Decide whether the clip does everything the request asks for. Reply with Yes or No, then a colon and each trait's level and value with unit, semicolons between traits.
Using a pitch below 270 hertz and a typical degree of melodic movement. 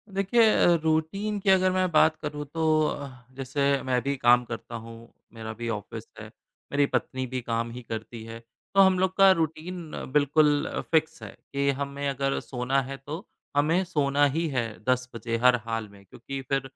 Yes: medium, 140 Hz; average, 4.7 semitones